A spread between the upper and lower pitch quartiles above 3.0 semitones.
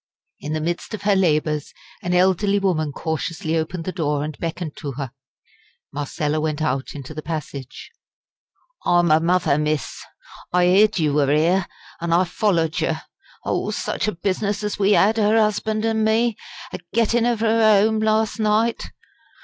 Yes: wide, 5.4 semitones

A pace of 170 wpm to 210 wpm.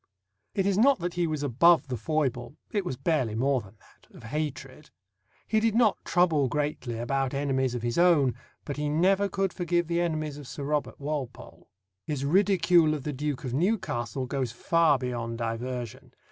Yes: average, 180 wpm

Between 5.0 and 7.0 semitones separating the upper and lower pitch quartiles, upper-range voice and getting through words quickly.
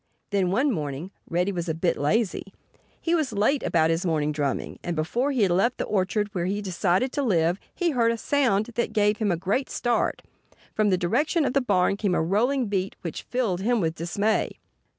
Yes: wide, 5.4 semitones; high, 200 Hz; fast, 210 wpm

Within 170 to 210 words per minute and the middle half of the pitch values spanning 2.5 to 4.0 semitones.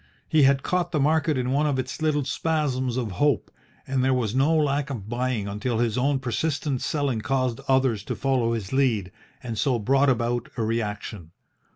Yes: average, 190 wpm; average, 3.4 semitones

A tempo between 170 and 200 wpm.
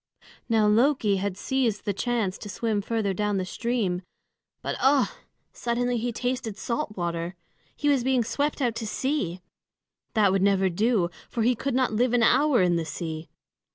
Yes: average, 175 wpm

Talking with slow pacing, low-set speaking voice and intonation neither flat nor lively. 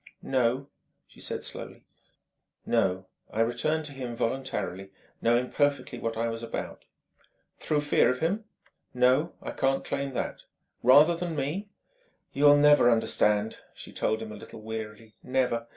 No: average, 150 wpm; low, 125 Hz; average, 4.2 semitones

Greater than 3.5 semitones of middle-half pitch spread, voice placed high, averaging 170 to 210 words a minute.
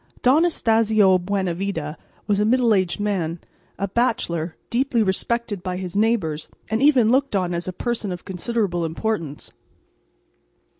No: average, 4.7 semitones; high, 200 Hz; average, 140 wpm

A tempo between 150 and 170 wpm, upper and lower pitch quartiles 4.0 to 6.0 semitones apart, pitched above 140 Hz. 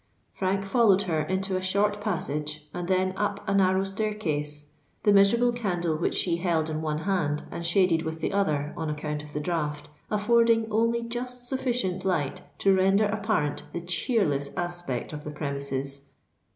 Yes: average, 165 wpm; average, 5.1 semitones; medium, 185 Hz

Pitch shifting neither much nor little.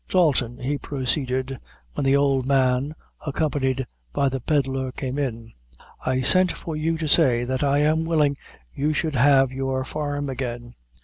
No: narrow, 2.2 semitones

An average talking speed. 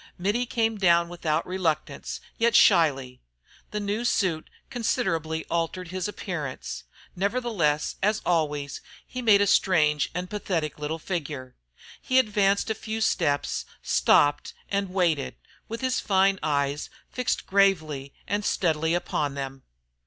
No: slow, 130 wpm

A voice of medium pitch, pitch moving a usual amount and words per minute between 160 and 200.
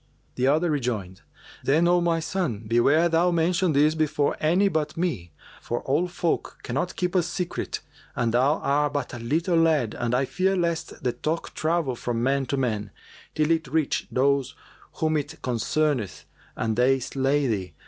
Yes: medium, 145 Hz; average, 5.0 semitones; average, 170 wpm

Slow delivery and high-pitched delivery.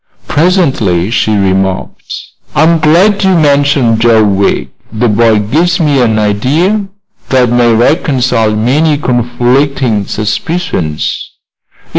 No: slow, 105 wpm; low, 125 Hz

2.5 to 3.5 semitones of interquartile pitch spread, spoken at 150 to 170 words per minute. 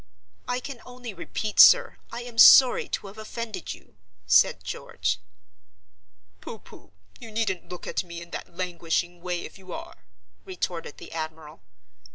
No: average, 5.0 semitones; average, 155 wpm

